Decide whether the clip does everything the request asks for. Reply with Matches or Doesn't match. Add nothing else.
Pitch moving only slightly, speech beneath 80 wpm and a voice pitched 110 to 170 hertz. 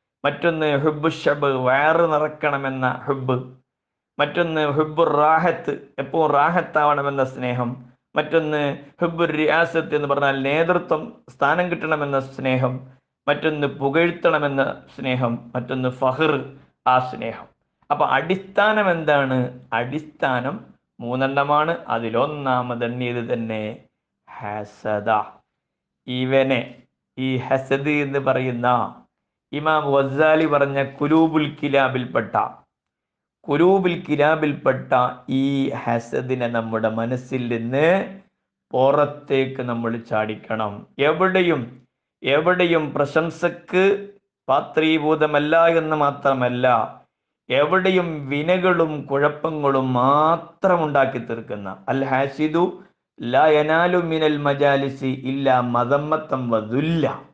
Doesn't match